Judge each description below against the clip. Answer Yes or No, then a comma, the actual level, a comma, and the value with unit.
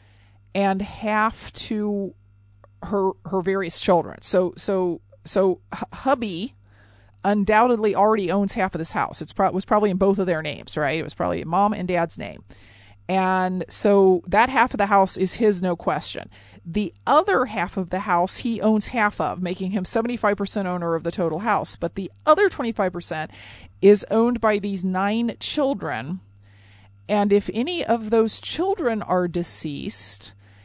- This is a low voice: No, high, 190 Hz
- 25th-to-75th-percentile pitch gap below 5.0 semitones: Yes, average, 3.9 semitones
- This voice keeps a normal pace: Yes, average, 160 wpm